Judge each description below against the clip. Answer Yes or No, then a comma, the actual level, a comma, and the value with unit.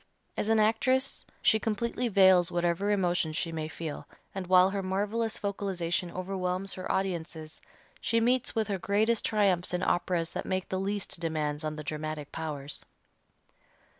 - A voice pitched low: No, medium, 185 Hz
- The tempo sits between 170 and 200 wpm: No, average, 155 wpm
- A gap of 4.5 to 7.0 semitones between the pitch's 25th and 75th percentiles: No, average, 3.7 semitones